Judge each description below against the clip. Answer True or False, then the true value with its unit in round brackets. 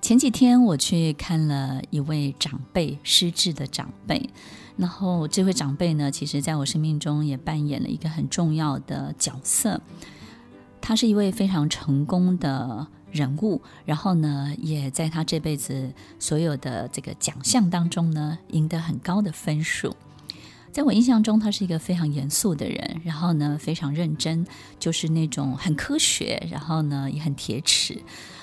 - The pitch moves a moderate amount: True (3.6 semitones)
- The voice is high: False (155 Hz)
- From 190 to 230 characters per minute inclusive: False (245 characters per minute)